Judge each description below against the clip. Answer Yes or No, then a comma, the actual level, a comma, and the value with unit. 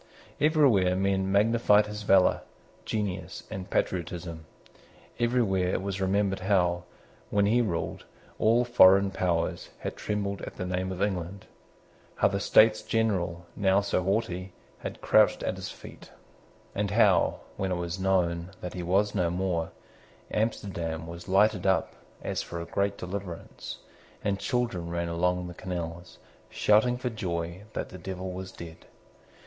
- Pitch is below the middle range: Yes, very low, 95 Hz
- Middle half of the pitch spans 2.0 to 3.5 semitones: Yes, average, 2.7 semitones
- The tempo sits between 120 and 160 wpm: Yes, average, 145 wpm